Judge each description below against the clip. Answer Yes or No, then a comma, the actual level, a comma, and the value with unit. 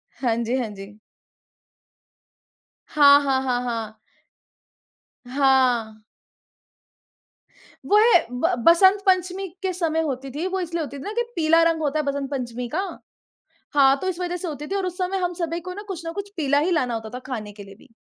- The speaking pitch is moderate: No, very high, 295 Hz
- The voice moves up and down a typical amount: No, wide, 6.1 semitones